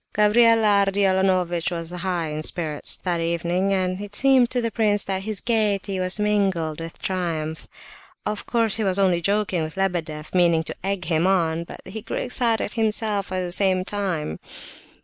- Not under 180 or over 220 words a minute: No, average, 170 wpm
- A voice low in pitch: No, high, 190 Hz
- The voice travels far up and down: No, average, 3.4 semitones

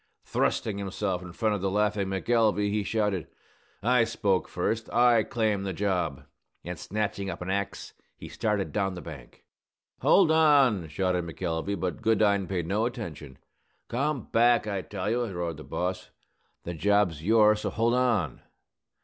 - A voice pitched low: Yes, low, 100 Hz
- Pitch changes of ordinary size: Yes, average, 3.6 semitones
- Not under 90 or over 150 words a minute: No, average, 160 wpm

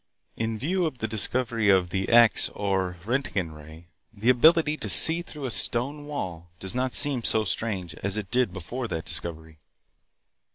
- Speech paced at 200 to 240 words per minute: No, average, 170 wpm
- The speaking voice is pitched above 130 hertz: No, low, 110 Hz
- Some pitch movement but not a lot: No, wide, 5.9 semitones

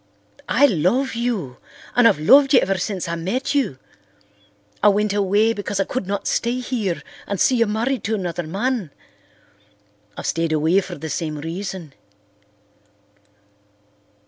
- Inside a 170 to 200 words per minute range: No, average, 145 wpm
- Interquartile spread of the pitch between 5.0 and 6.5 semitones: Yes, wide, 5.6 semitones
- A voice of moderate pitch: No, high, 200 Hz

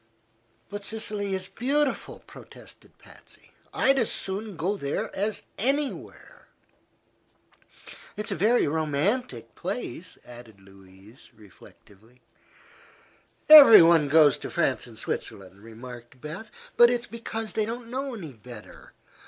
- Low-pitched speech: No, medium, 185 Hz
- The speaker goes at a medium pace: No, slow, 115 wpm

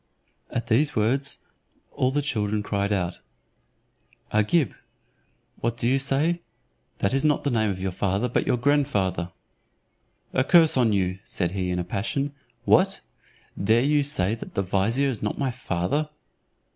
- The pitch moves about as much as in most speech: No, wide, 6.1 semitones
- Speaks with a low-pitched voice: Yes, low, 115 Hz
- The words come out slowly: No, average, 160 wpm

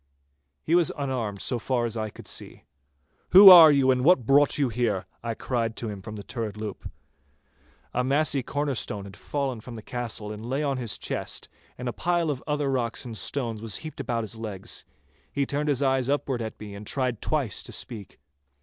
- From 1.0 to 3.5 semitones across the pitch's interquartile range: No, average, 4.2 semitones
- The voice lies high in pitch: No, low, 125 Hz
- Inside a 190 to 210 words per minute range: Yes, average, 200 wpm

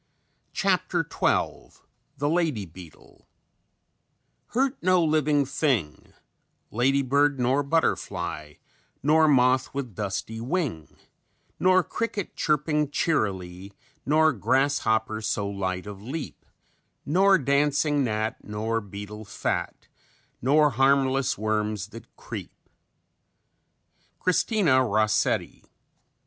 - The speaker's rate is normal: No, slow, 90 wpm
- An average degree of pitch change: No, wide, 6.0 semitones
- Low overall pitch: Yes, low, 130 Hz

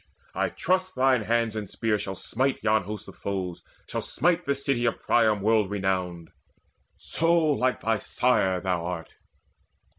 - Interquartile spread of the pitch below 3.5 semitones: No, average, 5.3 semitones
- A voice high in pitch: No, low, 110 Hz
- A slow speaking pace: No, average, 155 wpm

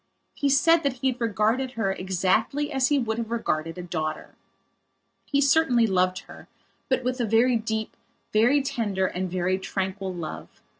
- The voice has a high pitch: Yes, high, 225 Hz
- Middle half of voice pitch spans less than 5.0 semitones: No, wide, 5.5 semitones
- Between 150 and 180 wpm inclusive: Yes, average, 165 wpm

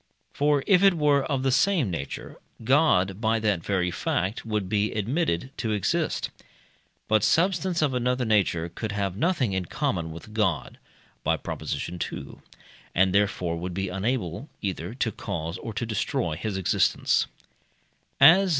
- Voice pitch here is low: Yes, low, 105 Hz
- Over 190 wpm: No, average, 150 wpm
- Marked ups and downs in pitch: Yes, wide, 6.1 semitones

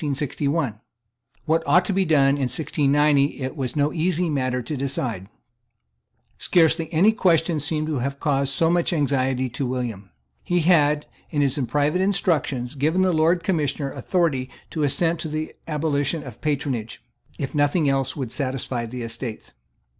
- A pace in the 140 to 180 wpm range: Yes, average, 155 wpm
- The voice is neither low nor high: Yes, medium, 145 Hz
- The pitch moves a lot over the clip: No, average, 3.5 semitones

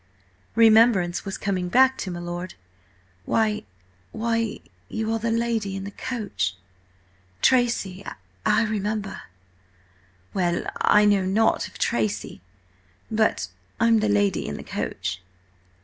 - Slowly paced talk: Yes, slow, 105 wpm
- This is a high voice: Yes, high, 195 Hz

